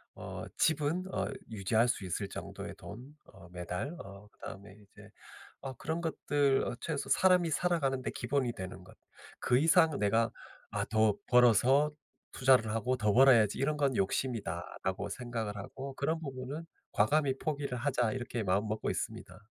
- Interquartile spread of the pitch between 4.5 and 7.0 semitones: Yes, wide, 5.6 semitones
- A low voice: Yes, low, 125 Hz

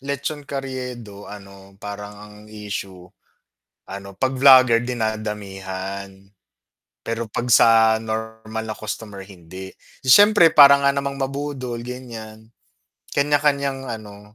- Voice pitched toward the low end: Yes, low, 110 Hz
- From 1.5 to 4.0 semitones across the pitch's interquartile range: No, average, 4.5 semitones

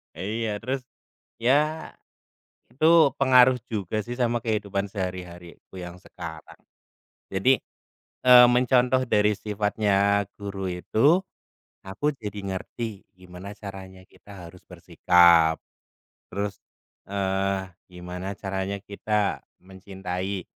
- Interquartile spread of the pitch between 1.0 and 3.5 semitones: No, average, 3.9 semitones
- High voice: No, low, 100 Hz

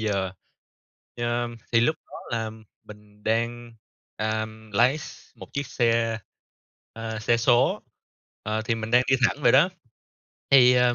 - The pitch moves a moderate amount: No, narrow, 1.8 semitones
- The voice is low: Yes, low, 115 Hz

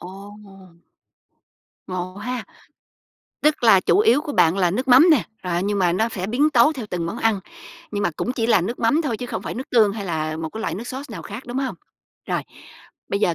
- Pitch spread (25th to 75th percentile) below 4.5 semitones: No, average, 5.3 semitones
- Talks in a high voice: Yes, high, 220 Hz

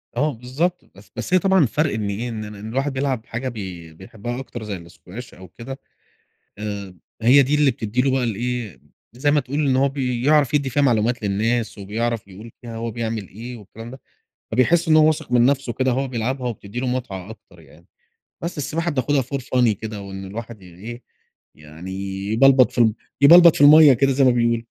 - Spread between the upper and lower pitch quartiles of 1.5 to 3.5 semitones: No, average, 4.0 semitones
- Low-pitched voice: Yes, low, 120 Hz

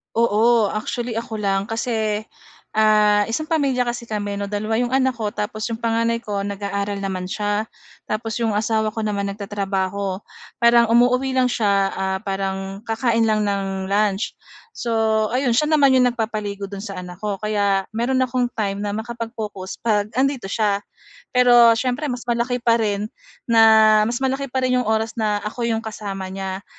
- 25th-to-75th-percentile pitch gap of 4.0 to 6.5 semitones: No, average, 2.8 semitones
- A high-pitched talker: Yes, high, 220 Hz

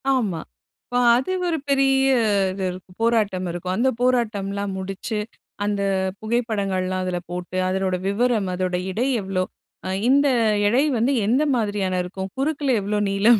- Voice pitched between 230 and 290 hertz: No, high, 205 Hz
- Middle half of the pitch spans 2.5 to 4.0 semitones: No, average, 4.5 semitones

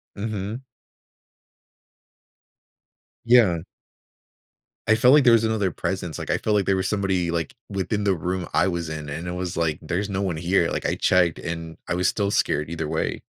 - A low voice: Yes, very low, 90 Hz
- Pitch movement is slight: No, average, 3.2 semitones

